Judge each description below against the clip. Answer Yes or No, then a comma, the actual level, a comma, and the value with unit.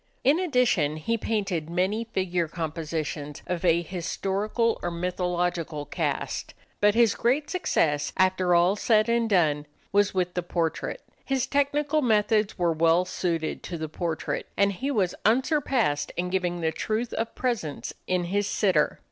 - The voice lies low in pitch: No, medium, 185 Hz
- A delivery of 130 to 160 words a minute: Yes, average, 150 wpm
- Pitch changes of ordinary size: Yes, average, 5.0 semitones